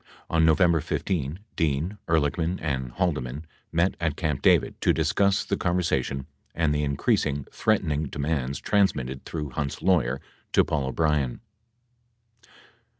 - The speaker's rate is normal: No, slow, 125 wpm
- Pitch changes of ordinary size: Yes, average, 3.6 semitones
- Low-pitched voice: Yes, very low, 75 Hz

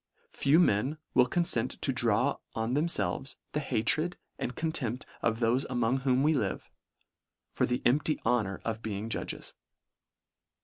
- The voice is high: No, low, 125 Hz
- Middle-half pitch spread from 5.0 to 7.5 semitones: No, average, 4.6 semitones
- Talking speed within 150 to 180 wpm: No, average, 140 wpm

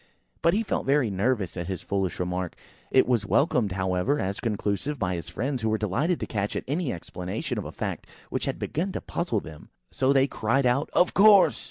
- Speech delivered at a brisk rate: Yes, fast, 210 wpm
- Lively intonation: Yes, wide, 7.0 semitones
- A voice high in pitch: No, low, 115 Hz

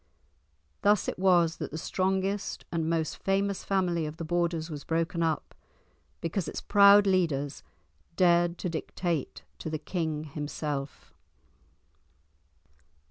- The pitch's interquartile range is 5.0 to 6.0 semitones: No, average, 3.1 semitones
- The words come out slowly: Yes, slow, 125 wpm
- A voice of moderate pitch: Yes, medium, 170 Hz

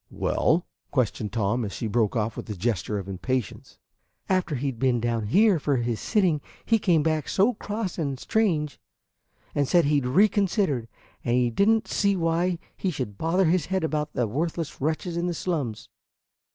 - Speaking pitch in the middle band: Yes, medium, 150 Hz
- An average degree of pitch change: No, wide, 7.1 semitones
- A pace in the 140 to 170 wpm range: No, average, 185 wpm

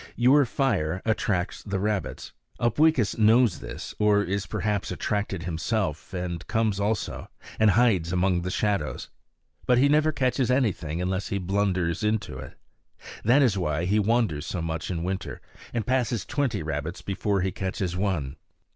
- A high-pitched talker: No, low, 100 Hz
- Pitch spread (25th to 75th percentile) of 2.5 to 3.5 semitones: No, average, 4.2 semitones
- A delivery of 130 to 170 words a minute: Yes, average, 155 wpm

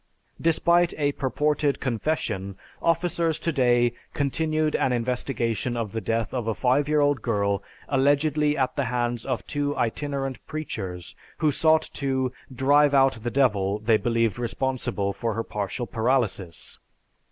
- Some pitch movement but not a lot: Yes, average, 4.2 semitones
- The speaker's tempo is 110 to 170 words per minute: Yes, average, 140 wpm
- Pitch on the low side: Yes, low, 130 Hz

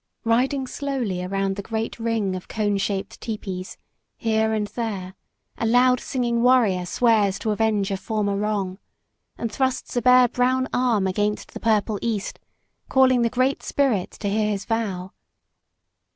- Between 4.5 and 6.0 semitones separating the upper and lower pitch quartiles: No, average, 3.5 semitones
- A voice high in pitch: Yes, high, 220 Hz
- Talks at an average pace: Yes, average, 150 wpm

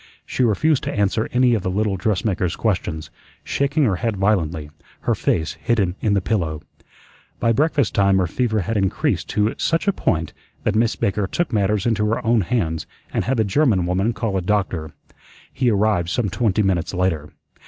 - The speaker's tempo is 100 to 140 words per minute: No, average, 185 wpm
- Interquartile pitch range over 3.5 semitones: Yes, average, 3.9 semitones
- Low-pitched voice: Yes, low, 105 Hz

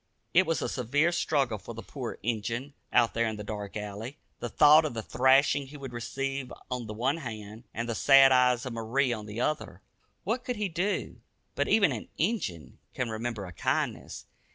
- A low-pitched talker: Yes, low, 125 Hz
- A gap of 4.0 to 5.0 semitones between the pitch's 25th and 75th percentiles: Yes, average, 4.6 semitones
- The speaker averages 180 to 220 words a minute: Yes, average, 200 wpm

